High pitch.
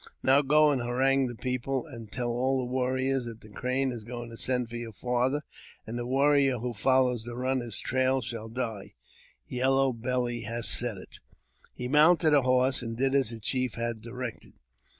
No: low, 125 Hz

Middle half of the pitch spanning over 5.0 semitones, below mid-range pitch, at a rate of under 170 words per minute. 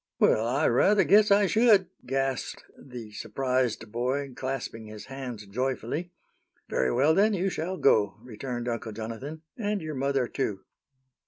Yes: wide, 5.4 semitones; low, 130 Hz; average, 145 wpm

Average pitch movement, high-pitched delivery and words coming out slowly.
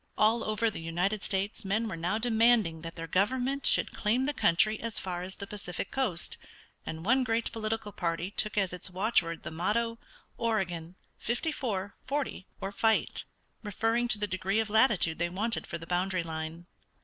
No: average, 4.3 semitones; high, 205 Hz; average, 180 wpm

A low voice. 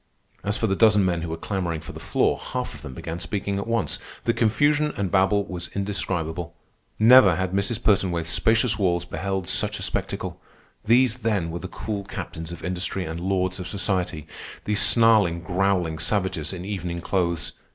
Yes: very low, 95 Hz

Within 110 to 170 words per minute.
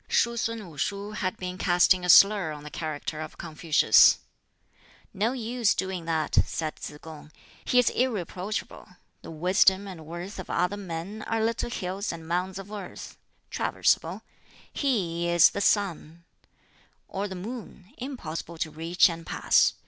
Yes: average, 155 wpm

